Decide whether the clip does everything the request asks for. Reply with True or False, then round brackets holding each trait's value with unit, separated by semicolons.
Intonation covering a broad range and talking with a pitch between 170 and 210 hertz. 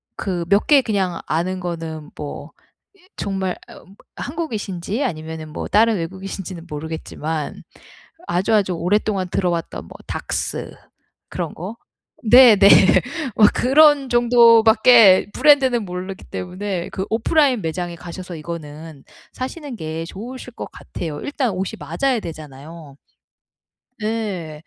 True (5.7 semitones; 190 Hz)